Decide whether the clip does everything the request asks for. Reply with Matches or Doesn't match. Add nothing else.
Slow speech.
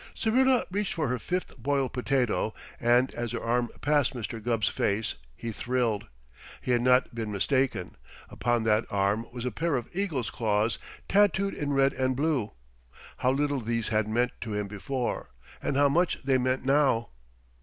Doesn't match